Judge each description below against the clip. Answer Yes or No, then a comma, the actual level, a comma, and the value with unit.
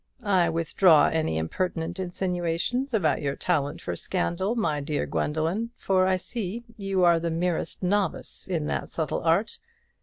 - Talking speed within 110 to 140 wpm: No, average, 150 wpm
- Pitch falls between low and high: Yes, medium, 175 Hz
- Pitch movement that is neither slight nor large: Yes, average, 3.1 semitones